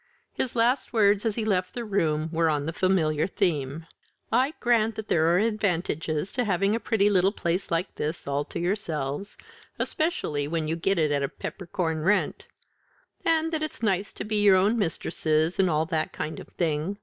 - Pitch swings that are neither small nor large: Yes, average, 5.0 semitones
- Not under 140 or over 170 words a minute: No, average, 190 wpm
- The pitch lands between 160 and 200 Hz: Yes, medium, 185 Hz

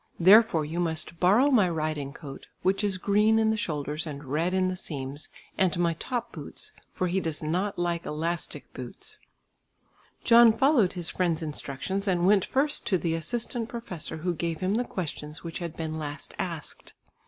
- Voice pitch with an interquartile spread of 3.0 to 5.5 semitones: Yes, average, 4.3 semitones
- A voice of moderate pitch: Yes, medium, 175 Hz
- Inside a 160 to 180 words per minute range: Yes, average, 175 wpm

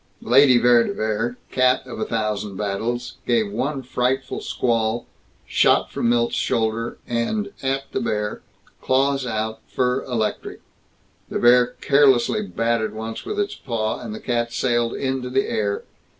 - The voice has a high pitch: No, low, 120 Hz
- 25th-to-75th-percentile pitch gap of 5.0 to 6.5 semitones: No, average, 2.8 semitones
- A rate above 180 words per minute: No, average, 150 wpm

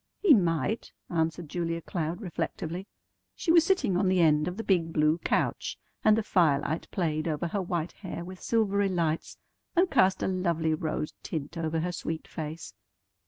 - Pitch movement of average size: Yes, average, 3.1 semitones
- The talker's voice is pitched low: No, medium, 170 Hz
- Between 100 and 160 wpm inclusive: No, average, 170 wpm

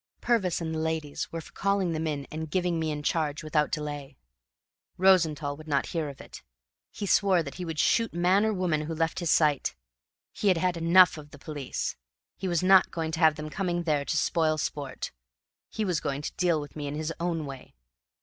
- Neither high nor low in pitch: Yes, medium, 160 Hz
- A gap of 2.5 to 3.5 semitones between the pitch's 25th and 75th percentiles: Yes, average, 3.0 semitones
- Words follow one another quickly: Yes, fast, 215 wpm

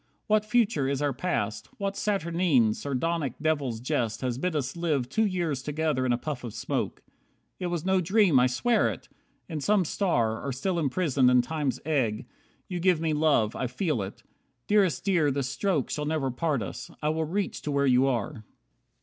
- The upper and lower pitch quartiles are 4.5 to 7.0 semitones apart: Yes, wide, 5.6 semitones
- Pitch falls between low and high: Yes, medium, 150 Hz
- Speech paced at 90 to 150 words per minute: No, average, 190 wpm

